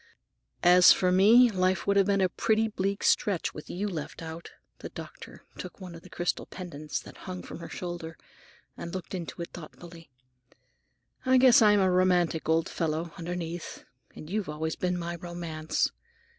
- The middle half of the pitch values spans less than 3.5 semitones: Yes, narrow, 2.4 semitones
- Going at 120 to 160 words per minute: No, average, 170 wpm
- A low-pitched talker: No, medium, 175 Hz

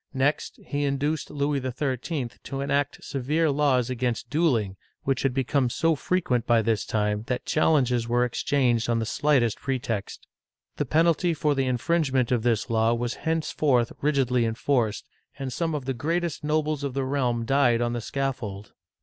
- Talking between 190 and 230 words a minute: No, average, 165 wpm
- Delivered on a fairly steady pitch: No, average, 3.6 semitones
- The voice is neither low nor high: No, low, 130 Hz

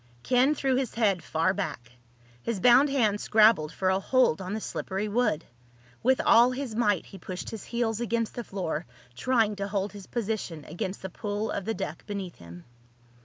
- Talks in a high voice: Yes, high, 210 Hz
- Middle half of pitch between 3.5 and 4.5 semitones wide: Yes, average, 4.0 semitones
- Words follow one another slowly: No, average, 185 wpm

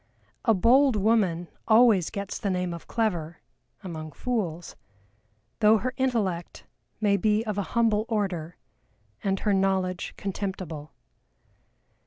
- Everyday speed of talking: No, slow, 120 wpm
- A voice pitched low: No, high, 200 Hz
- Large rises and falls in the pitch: No, average, 3.8 semitones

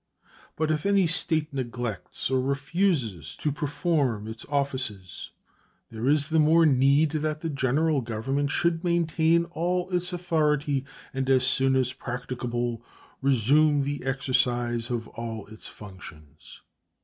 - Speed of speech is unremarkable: No, slow, 130 wpm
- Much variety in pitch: No, average, 4.4 semitones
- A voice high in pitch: No, medium, 140 Hz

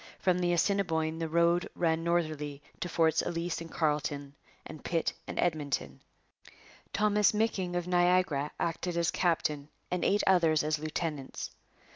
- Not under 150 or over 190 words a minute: No, average, 140 wpm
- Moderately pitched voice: Yes, medium, 165 Hz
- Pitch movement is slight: Yes, narrow, 2.2 semitones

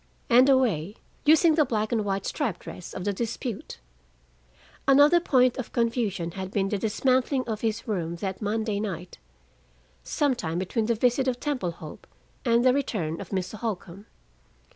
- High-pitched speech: Yes, high, 220 Hz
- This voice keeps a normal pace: Yes, average, 165 wpm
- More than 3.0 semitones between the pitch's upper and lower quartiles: Yes, average, 4.9 semitones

